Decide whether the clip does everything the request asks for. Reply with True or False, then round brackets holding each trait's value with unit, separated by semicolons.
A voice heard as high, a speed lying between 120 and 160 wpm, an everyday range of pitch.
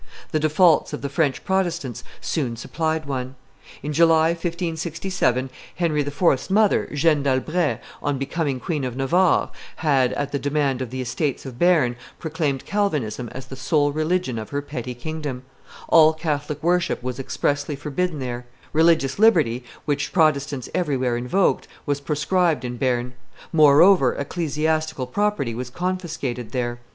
False (145 Hz; 140 wpm; 4.1 semitones)